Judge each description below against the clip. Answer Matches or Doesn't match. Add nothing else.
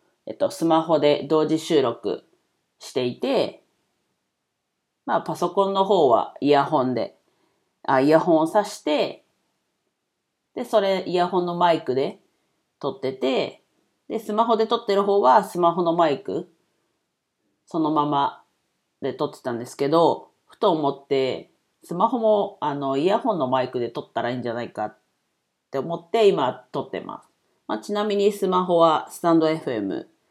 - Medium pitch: Matches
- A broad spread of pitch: Matches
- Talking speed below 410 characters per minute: Matches